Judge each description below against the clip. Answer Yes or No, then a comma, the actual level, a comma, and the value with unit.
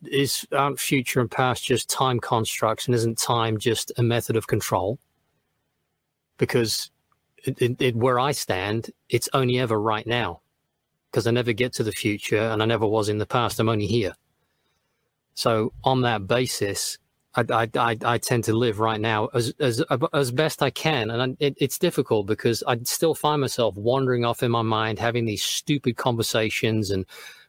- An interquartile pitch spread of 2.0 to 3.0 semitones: Yes, narrow, 2.6 semitones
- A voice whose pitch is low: Yes, low, 120 Hz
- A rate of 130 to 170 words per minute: No, average, 185 wpm